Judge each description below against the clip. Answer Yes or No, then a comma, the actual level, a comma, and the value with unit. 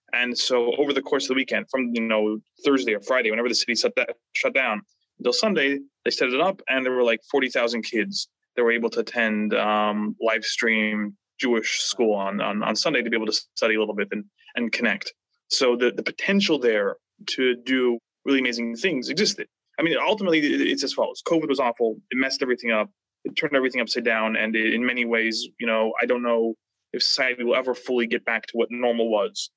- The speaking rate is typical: No, fast, 215 wpm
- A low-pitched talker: Yes, low, 120 Hz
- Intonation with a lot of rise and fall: No, average, 2.9 semitones